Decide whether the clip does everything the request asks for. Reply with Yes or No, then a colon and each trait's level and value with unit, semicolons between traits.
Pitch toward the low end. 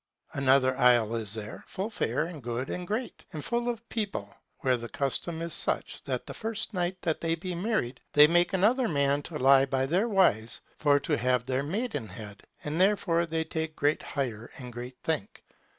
No: medium, 150 Hz